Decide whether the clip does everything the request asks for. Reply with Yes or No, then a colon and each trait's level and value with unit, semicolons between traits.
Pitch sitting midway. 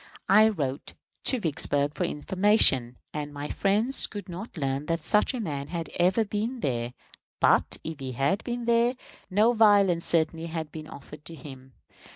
Yes: medium, 165 Hz